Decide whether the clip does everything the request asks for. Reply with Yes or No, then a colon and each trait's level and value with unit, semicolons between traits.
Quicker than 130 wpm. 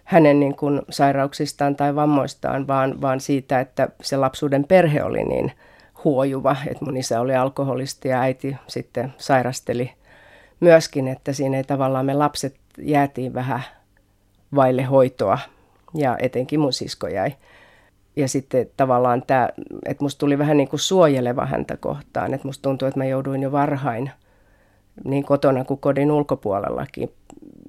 Yes: average, 145 wpm